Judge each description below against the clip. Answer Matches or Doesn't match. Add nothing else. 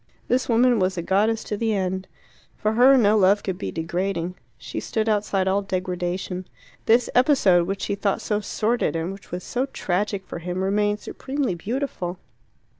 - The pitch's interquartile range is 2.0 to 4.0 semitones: Matches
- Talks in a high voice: Matches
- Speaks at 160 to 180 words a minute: Matches